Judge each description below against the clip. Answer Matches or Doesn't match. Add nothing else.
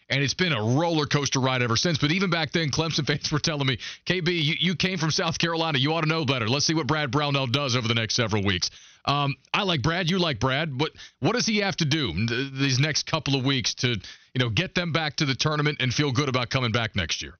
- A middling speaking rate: Doesn't match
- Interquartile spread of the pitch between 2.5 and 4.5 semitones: Matches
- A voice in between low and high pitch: Matches